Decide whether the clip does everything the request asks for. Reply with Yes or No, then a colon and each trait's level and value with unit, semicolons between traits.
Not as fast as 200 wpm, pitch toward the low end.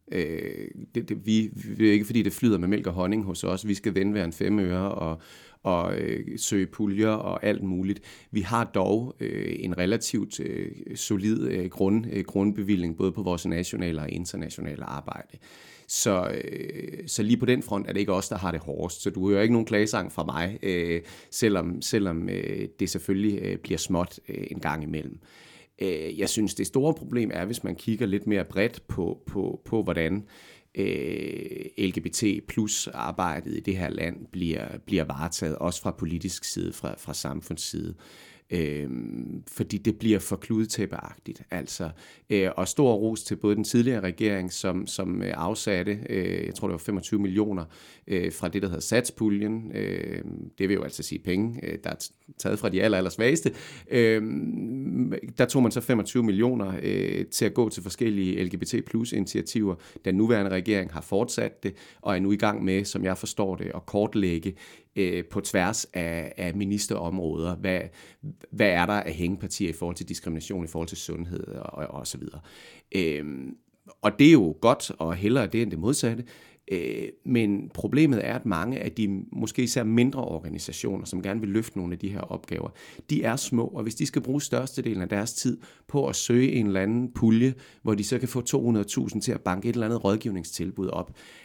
Yes: average, 185 wpm; low, 100 Hz